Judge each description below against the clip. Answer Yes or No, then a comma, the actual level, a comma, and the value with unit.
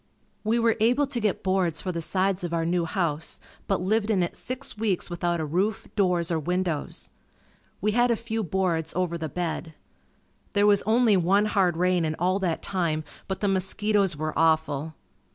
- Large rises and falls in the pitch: No, average, 3.8 semitones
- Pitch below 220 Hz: Yes, medium, 185 Hz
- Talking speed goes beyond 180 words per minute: Yes, average, 190 wpm